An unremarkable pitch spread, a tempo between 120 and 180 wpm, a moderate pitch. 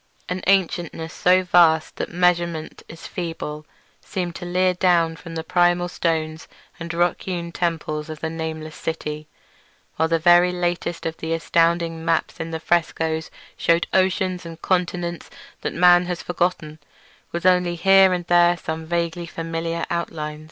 No: narrow, 1.5 semitones; average, 150 wpm; medium, 170 Hz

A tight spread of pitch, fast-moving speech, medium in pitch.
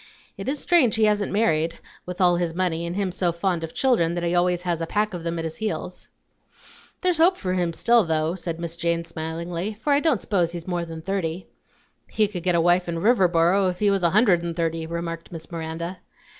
No: average, 3.0 semitones; fast, 225 wpm; medium, 175 Hz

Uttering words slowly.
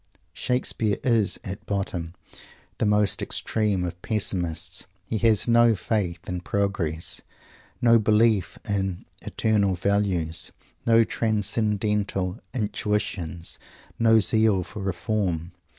Yes: slow, 105 wpm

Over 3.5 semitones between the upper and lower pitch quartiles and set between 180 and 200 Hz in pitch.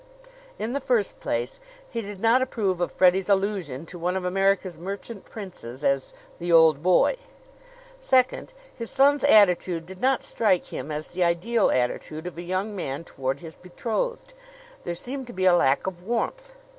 Yes: average, 5.2 semitones; high, 190 Hz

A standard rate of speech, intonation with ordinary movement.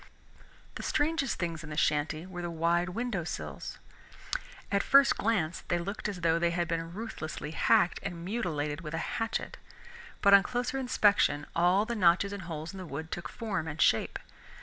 Yes: average, 175 wpm; average, 4.0 semitones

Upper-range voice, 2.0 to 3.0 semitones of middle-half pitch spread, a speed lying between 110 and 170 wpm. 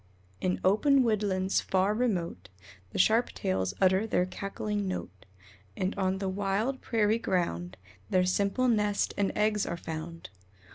Yes: high, 195 Hz; narrow, 2.6 semitones; average, 140 wpm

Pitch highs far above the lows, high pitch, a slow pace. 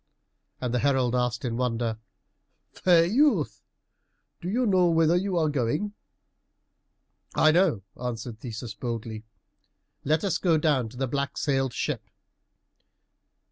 No: wide, 6.1 semitones; low, 135 Hz; slow, 130 wpm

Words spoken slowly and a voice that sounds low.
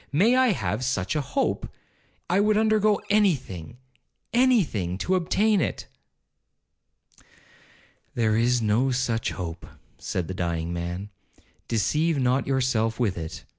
Yes: slow, 130 wpm; low, 125 Hz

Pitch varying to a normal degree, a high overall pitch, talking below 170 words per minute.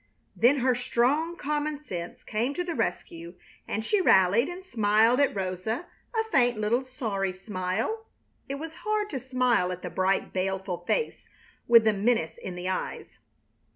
No: wide, 7.0 semitones; high, 235 Hz; average, 160 wpm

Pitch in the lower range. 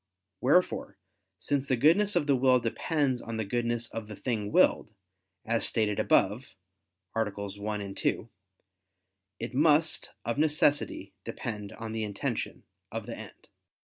Yes: low, 115 Hz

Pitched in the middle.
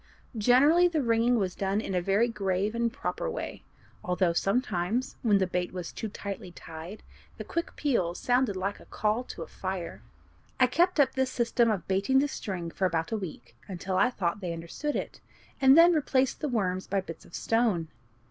No: high, 205 Hz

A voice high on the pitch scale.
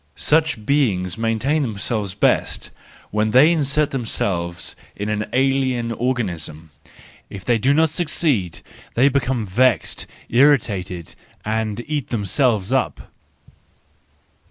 No: low, 115 Hz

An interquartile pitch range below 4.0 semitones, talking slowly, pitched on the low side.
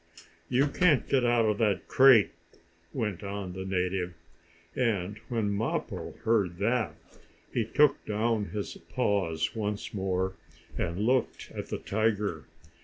Yes: average, 3.6 semitones; slow, 130 wpm; low, 105 Hz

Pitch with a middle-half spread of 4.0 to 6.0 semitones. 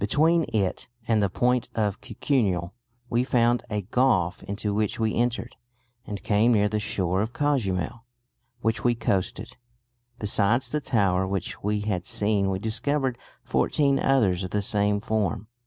No: average, 3.5 semitones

